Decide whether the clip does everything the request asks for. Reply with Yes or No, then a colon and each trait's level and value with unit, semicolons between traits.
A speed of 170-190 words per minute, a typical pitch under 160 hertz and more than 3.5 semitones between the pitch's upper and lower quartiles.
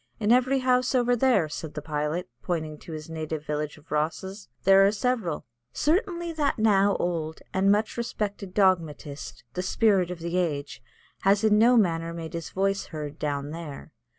No: average, 175 wpm; medium, 185 Hz; wide, 5.5 semitones